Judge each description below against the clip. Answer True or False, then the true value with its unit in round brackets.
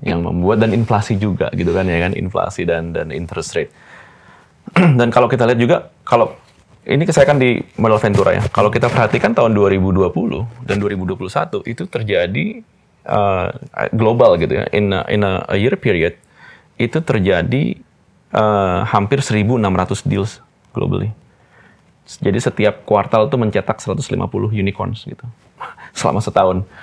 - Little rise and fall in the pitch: False (3.9 semitones)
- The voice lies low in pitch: True (110 Hz)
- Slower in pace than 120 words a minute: False (140 wpm)